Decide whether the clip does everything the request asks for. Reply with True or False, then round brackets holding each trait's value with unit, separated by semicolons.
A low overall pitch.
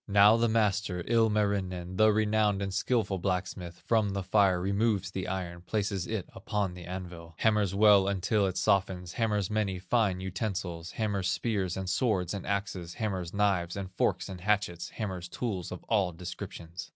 True (95 Hz)